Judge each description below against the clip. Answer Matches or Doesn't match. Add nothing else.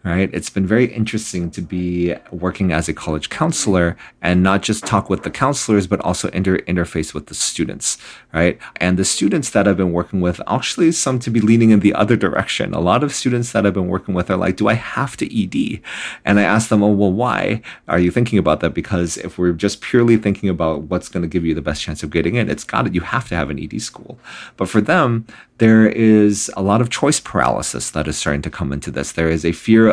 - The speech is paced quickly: Matches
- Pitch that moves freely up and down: Doesn't match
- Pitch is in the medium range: Doesn't match